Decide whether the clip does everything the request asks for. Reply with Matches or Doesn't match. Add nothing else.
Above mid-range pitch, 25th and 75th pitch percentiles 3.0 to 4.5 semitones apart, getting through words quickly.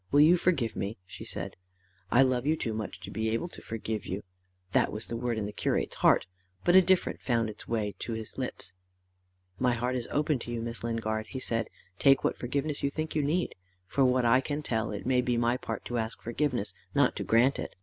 Doesn't match